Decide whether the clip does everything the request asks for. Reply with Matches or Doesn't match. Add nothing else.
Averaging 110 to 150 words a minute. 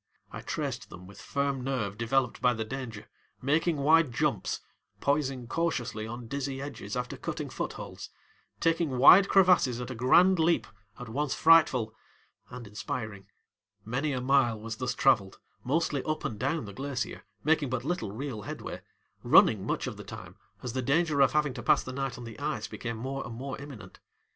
Doesn't match